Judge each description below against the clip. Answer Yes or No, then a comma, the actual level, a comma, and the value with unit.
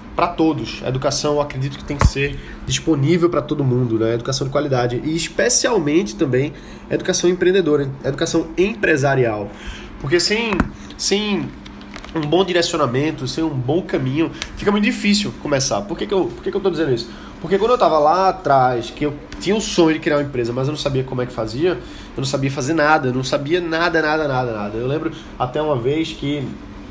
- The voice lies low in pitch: No, medium, 150 Hz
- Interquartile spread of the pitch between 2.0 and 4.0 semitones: No, average, 4.5 semitones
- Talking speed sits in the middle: No, fast, 205 wpm